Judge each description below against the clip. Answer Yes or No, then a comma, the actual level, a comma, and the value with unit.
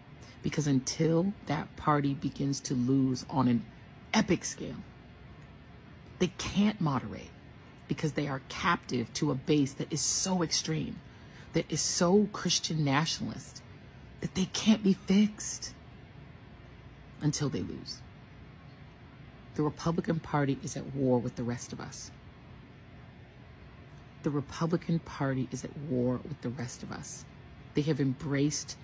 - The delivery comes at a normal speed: No, slow, 130 wpm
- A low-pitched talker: No, medium, 145 Hz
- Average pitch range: Yes, average, 3.8 semitones